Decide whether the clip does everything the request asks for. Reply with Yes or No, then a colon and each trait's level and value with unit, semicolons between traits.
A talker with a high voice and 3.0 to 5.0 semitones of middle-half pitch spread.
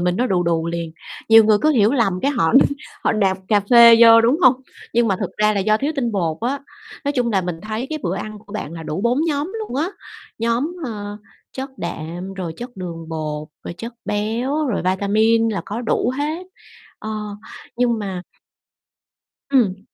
Yes: high, 215 Hz; average, 4.7 semitones